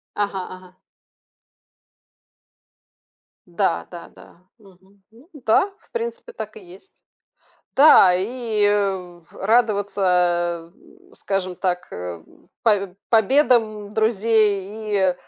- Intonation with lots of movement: No, average, 3.8 semitones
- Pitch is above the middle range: Yes, high, 200 Hz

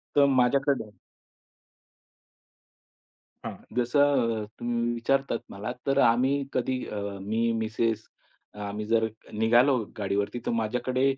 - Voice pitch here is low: Yes, low, 120 Hz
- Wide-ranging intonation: No, average, 2.9 semitones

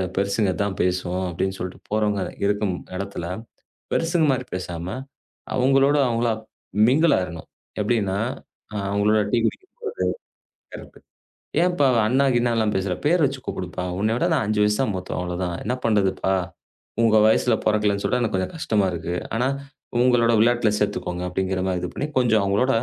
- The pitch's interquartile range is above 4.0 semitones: Yes, average, 4.5 semitones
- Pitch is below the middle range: Yes, low, 105 Hz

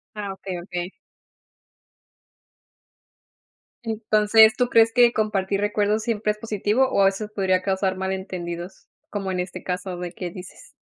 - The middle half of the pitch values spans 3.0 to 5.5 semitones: No, narrow, 2.4 semitones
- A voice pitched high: Yes, high, 200 Hz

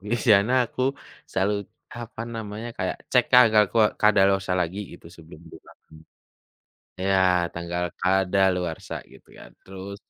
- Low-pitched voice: Yes, very low, 95 Hz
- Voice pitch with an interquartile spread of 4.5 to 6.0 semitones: No, average, 2.8 semitones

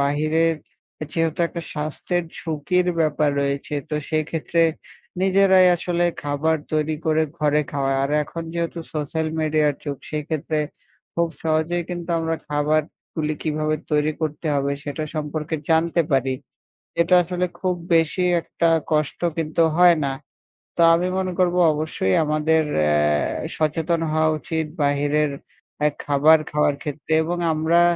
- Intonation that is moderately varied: No, narrow, 1.9 semitones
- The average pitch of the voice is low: No, medium, 155 Hz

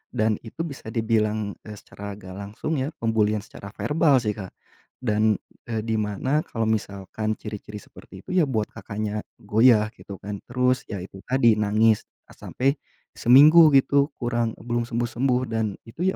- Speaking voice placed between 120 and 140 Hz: No, low, 110 Hz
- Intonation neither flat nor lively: Yes, average, 3.2 semitones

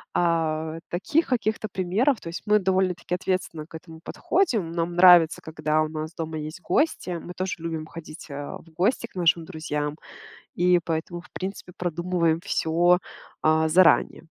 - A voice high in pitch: No, medium, 170 Hz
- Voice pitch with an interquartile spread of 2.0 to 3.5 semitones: Yes, narrow, 2.6 semitones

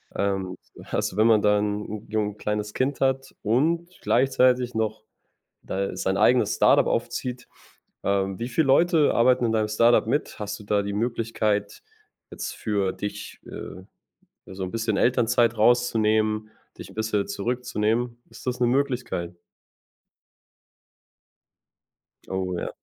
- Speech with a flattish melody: No, average, 3.2 semitones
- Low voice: Yes, low, 110 Hz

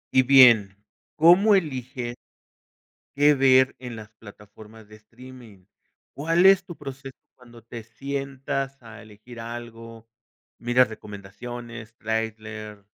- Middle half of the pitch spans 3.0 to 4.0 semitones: Yes, average, 3.3 semitones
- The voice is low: Yes, low, 120 Hz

